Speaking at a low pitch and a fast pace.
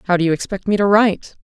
No: high, 190 Hz; fast, 295 wpm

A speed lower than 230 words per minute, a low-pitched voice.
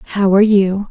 No: average, 200 wpm; high, 200 Hz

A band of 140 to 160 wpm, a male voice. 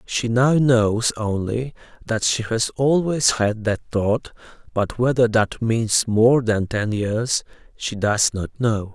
Yes: average, 155 wpm; male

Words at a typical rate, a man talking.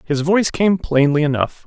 Yes: average, 180 wpm; male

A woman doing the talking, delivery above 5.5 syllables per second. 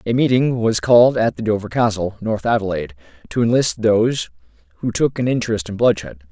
No: male; 5.9 syllables/s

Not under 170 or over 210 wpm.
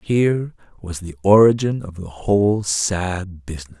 No: average, 140 wpm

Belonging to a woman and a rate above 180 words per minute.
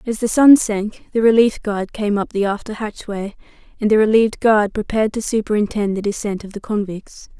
Yes: female; average, 195 wpm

